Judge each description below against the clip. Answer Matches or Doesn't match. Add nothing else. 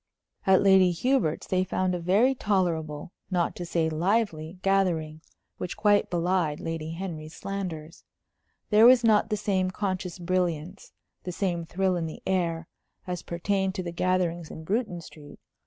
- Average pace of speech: Matches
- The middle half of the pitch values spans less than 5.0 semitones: Matches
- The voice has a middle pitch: Matches